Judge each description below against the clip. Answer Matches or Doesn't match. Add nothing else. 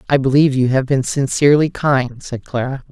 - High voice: Doesn't match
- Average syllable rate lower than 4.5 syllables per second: Doesn't match